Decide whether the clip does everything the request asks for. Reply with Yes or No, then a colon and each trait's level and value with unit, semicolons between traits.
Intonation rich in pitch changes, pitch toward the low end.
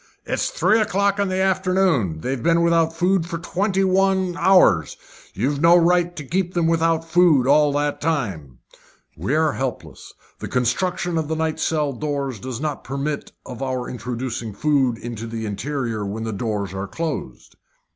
No: wide, 6.2 semitones; medium, 150 Hz